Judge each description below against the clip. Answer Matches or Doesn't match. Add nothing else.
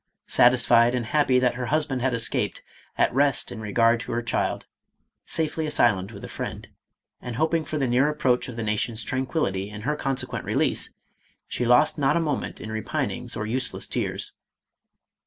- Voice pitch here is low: Matches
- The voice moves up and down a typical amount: Matches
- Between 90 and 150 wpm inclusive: Doesn't match